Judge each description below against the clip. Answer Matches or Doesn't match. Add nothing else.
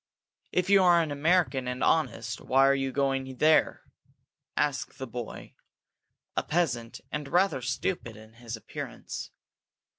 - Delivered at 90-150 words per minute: Matches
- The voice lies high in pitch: Doesn't match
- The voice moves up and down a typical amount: Matches